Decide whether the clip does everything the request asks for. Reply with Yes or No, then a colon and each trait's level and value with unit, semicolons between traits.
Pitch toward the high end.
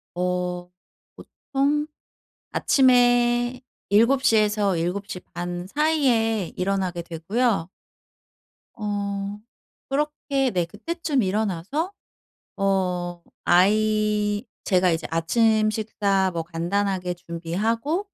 Yes: high, 205 Hz